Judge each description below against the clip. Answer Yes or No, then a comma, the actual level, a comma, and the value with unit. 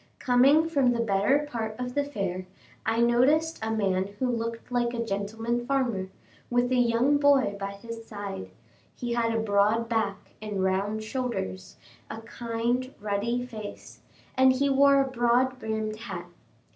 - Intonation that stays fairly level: No, average, 3.0 semitones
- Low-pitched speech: No, high, 235 Hz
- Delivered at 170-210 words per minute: No, average, 160 wpm